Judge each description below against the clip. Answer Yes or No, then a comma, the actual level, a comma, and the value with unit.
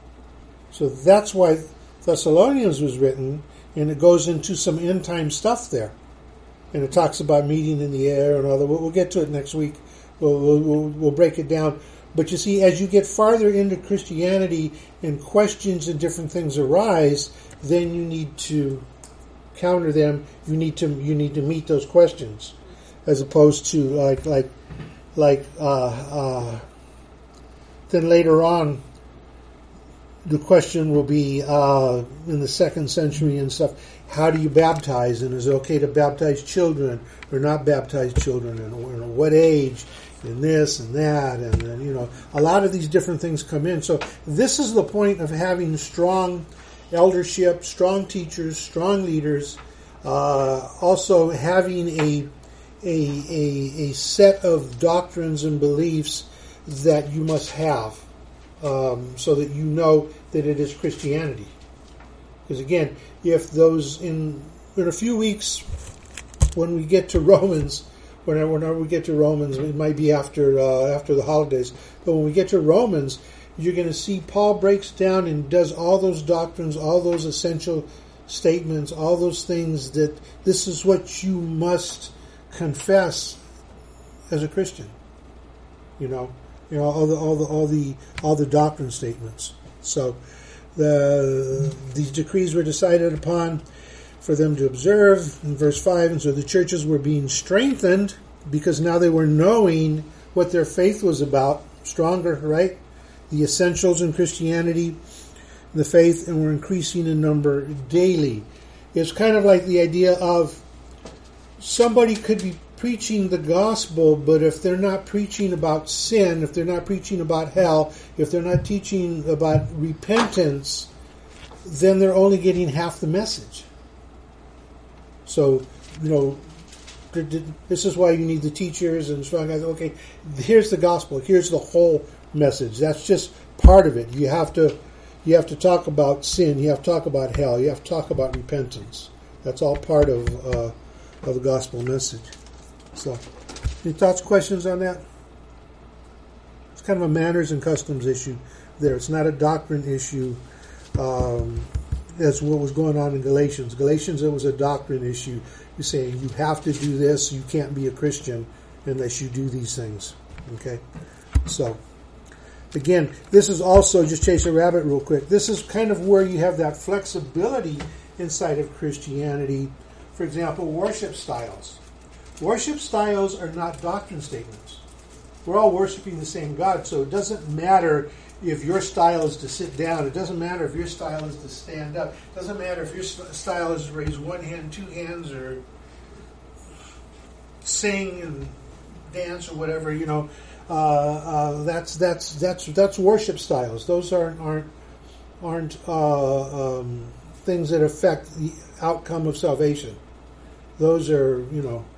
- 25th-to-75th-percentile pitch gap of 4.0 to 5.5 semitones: Yes, average, 4.3 semitones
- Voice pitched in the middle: Yes, medium, 155 Hz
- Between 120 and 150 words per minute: No, average, 160 wpm